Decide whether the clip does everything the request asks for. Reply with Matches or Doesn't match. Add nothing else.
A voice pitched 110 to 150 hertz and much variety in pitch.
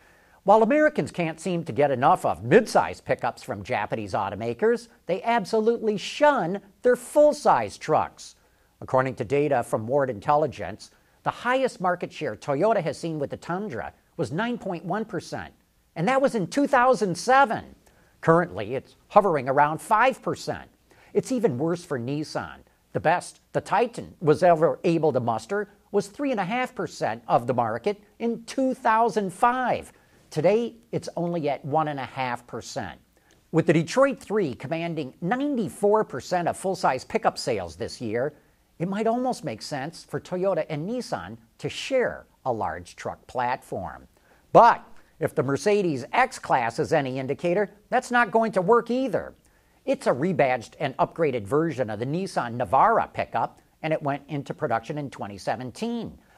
Doesn't match